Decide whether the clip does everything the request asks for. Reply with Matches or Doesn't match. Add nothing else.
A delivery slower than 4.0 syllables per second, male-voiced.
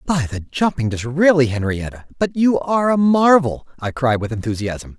Doesn't match